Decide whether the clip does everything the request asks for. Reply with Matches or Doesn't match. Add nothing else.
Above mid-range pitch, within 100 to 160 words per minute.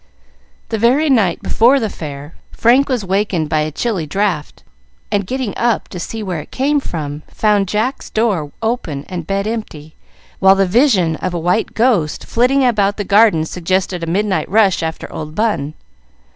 Doesn't match